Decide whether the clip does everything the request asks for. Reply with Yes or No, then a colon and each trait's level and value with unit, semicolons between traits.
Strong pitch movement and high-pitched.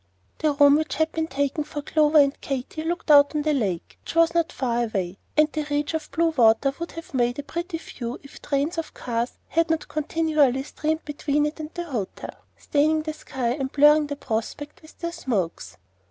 No: average, 2.9 semitones; very high, 295 Hz